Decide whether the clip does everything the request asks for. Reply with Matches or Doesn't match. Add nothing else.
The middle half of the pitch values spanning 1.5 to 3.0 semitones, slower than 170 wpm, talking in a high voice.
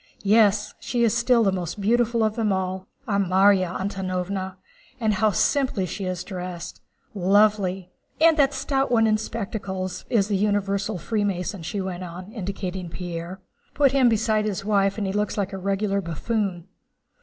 Matches